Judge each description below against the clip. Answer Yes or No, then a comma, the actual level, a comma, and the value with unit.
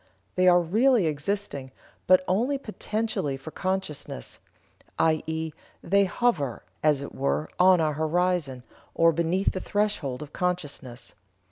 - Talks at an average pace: No, slow, 125 wpm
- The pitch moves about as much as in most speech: Yes, average, 4.3 semitones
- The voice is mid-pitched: Yes, medium, 170 Hz